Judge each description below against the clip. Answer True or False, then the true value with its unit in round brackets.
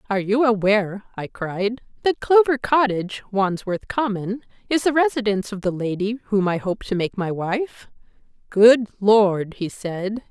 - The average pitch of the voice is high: True (215 Hz)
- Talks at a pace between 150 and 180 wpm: True (155 wpm)